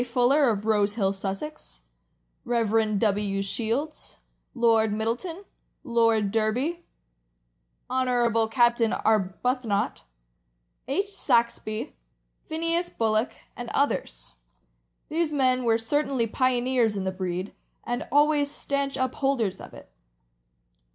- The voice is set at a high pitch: Yes, high, 235 Hz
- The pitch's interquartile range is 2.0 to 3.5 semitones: No, average, 4.0 semitones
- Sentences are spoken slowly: Yes, slow, 100 wpm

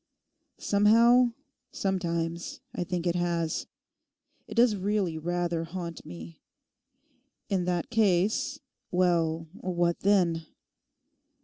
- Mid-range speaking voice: Yes, medium, 175 Hz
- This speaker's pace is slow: Yes, slow, 90 wpm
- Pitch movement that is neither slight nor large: Yes, average, 3.0 semitones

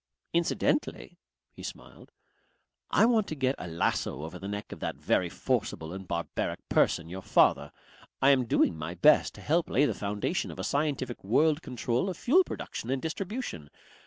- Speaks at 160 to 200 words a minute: Yes, average, 175 wpm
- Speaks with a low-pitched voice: Yes, low, 125 Hz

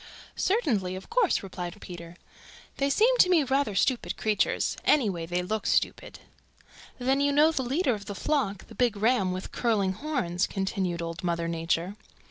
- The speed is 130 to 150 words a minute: No, average, 165 wpm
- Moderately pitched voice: No, high, 205 Hz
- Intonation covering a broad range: Yes, wide, 7.4 semitones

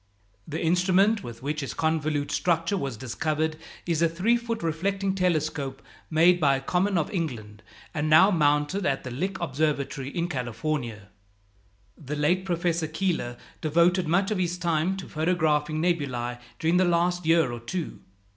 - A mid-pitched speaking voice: Yes, medium, 160 Hz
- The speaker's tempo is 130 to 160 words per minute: Yes, average, 155 wpm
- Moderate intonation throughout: Yes, average, 3.5 semitones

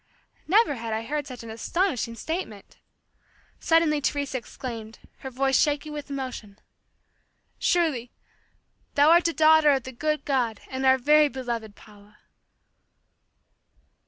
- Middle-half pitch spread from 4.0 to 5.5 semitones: Yes, average, 4.6 semitones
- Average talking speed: No, slow, 130 wpm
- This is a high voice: Yes, very high, 270 Hz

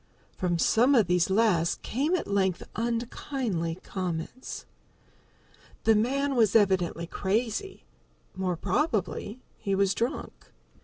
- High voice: Yes, high, 205 Hz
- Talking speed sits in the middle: No, slow, 110 wpm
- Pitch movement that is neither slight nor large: Yes, average, 4.7 semitones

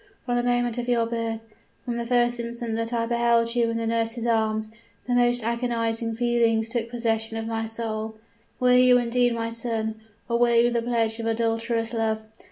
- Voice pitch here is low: No, high, 230 Hz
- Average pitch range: No, narrow, 1.1 semitones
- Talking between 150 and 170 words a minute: No, average, 190 wpm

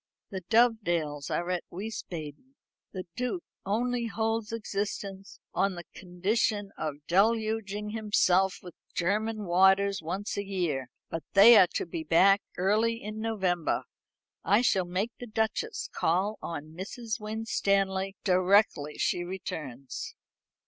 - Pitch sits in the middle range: No, high, 195 Hz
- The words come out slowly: Yes, slow, 125 wpm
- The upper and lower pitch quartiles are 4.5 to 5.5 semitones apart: No, average, 3.7 semitones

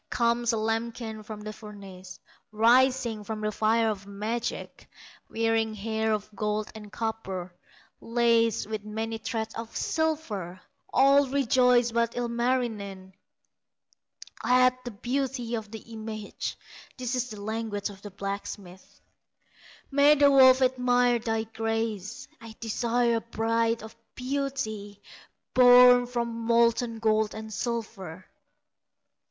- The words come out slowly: Yes, slow, 120 wpm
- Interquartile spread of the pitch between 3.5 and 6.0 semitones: No, narrow, 2.4 semitones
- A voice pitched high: Yes, high, 225 Hz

